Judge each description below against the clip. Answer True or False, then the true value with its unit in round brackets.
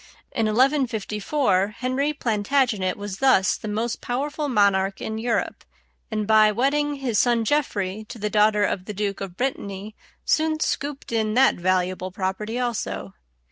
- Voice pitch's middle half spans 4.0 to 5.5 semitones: True (4.4 semitones)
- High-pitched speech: True (215 Hz)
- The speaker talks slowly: False (145 wpm)